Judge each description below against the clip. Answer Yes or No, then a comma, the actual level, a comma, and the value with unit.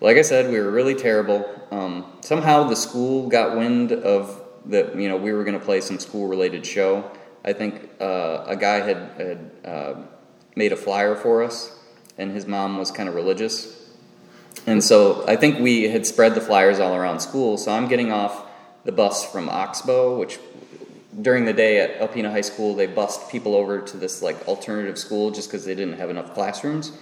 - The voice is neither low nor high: No, low, 105 Hz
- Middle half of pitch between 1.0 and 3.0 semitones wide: No, average, 4.0 semitones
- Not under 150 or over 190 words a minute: No, average, 200 wpm